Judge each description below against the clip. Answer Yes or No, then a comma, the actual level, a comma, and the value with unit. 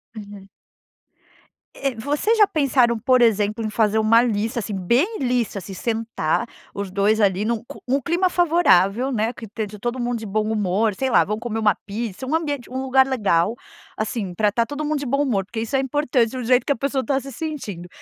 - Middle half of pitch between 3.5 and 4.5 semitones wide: Yes, average, 4.1 semitones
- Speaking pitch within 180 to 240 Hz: Yes, high, 235 Hz